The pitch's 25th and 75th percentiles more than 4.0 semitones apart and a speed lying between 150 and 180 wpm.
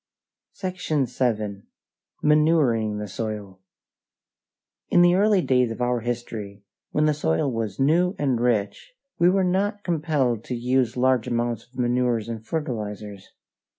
No: wide, 5.5 semitones; slow, 135 wpm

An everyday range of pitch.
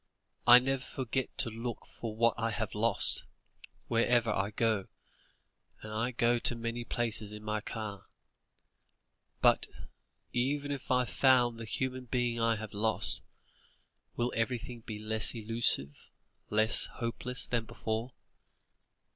No: narrow, 2.0 semitones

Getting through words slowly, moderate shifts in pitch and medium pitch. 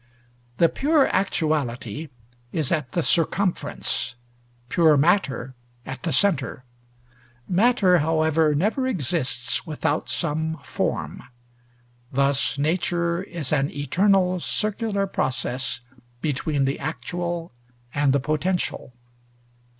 Yes: slow, 95 wpm; average, 4.3 semitones; medium, 160 Hz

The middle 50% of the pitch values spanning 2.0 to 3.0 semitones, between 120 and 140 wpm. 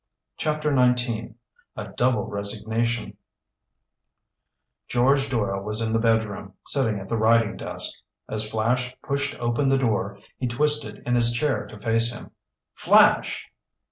Yes: average, 2.7 semitones; slow, 135 wpm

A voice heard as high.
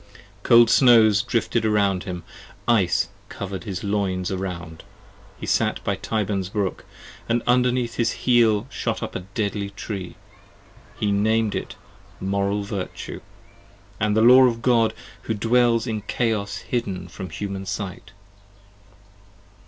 No: low, 105 Hz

